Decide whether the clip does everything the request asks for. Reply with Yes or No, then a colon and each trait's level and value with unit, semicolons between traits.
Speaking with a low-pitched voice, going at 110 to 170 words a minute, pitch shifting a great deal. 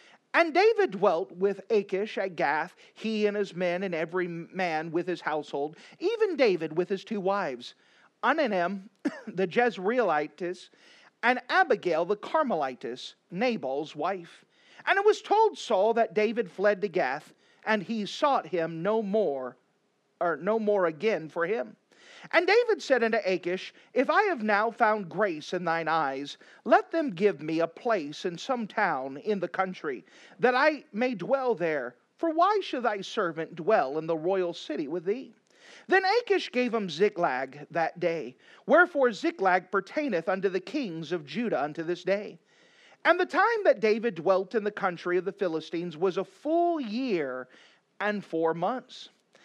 No: high, 205 Hz; average, 165 wpm; wide, 7.1 semitones